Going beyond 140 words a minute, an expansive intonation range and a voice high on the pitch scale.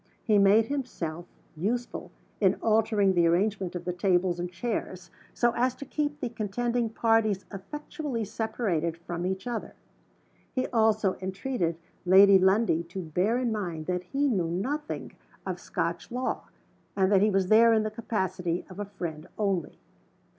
No: average, 155 wpm; average, 4.2 semitones; high, 200 Hz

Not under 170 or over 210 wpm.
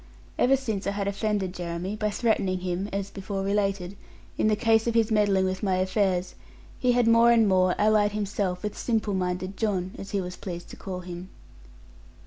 Yes: average, 185 wpm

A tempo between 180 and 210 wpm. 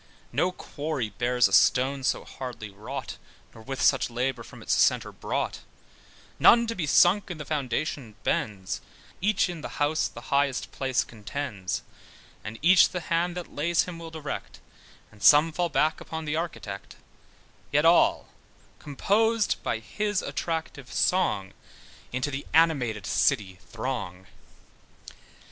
No: average, 140 wpm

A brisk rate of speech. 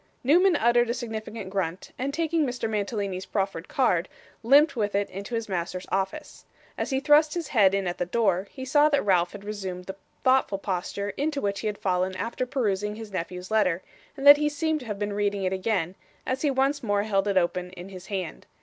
Yes: fast, 215 wpm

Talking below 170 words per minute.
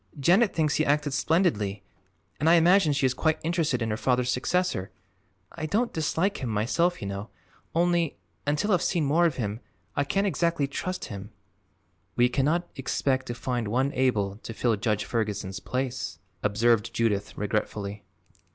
Yes: average, 160 wpm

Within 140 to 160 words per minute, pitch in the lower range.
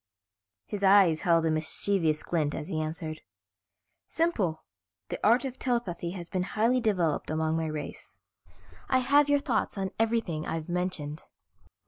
No: average, 145 wpm; medium, 180 Hz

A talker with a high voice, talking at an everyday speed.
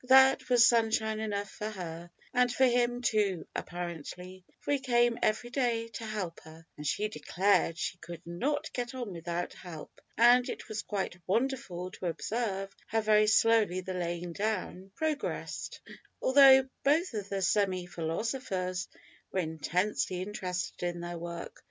Yes: high, 205 Hz; average, 150 wpm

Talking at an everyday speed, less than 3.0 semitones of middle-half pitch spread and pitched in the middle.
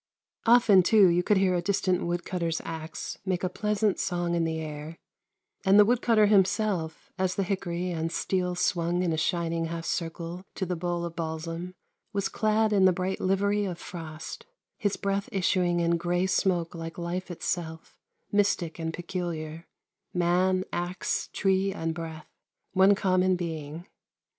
Yes: average, 160 wpm; narrow, 2.4 semitones; medium, 180 Hz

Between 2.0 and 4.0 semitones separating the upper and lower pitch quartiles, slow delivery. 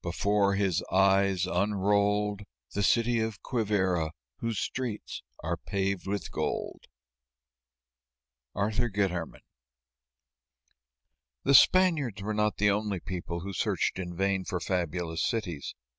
Yes: narrow, 2.6 semitones; slow, 115 wpm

